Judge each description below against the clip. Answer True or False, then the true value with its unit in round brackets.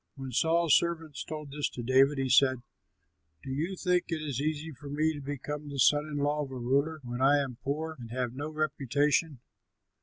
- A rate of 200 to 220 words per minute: True (205 wpm)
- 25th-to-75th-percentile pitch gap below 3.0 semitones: True (2.6 semitones)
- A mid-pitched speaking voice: True (145 Hz)